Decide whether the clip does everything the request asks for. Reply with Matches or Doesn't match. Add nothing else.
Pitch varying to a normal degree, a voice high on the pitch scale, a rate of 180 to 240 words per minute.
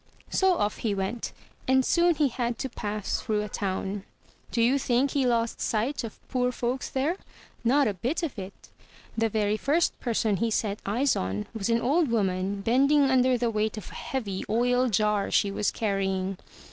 Matches